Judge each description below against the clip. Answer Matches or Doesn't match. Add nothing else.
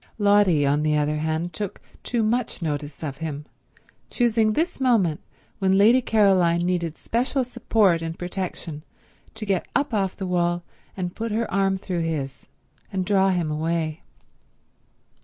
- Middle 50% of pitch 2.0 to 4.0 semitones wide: Doesn't match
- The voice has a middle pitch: Matches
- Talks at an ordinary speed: Matches